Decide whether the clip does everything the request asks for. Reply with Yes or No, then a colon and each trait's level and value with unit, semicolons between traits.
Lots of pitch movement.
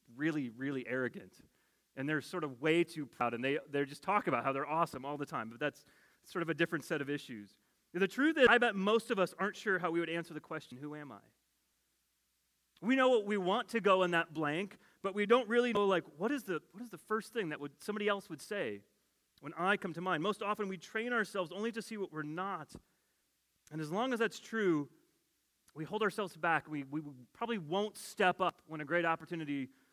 Yes: wide, 5.8 semitones